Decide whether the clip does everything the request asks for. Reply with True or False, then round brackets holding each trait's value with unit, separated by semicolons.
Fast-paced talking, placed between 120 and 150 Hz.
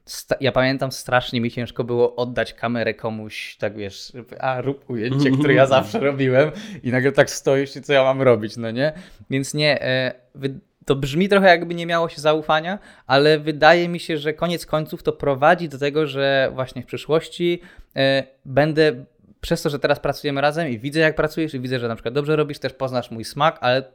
True (195 wpm; 140 Hz)